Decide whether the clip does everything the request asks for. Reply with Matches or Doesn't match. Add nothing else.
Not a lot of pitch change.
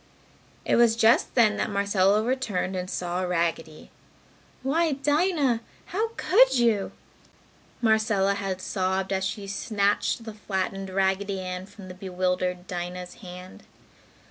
Doesn't match